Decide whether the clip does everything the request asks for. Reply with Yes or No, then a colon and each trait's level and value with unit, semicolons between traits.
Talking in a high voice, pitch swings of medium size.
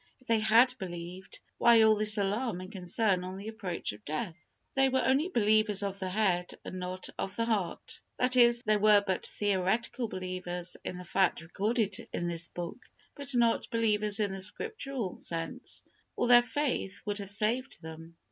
Yes: high, 205 Hz; average, 4.1 semitones